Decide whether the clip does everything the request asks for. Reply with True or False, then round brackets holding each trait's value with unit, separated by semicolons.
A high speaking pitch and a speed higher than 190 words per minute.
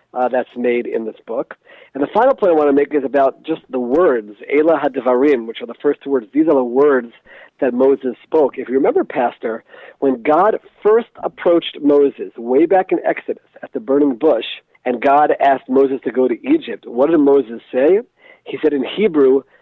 False (140 Hz; 205 wpm)